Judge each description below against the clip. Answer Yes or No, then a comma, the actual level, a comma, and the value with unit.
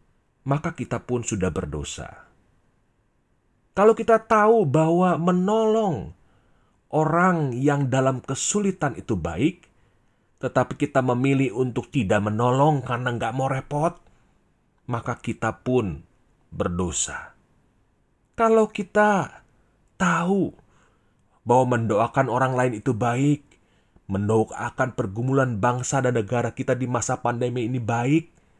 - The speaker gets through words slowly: No, average, 105 wpm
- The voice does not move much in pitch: No, average, 3.8 semitones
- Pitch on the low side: Yes, low, 130 Hz